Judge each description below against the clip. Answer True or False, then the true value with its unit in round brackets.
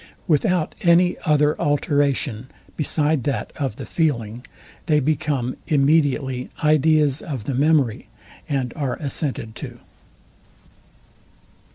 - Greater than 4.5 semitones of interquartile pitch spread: False (3.0 semitones)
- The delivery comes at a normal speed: False (100 wpm)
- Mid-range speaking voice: True (145 Hz)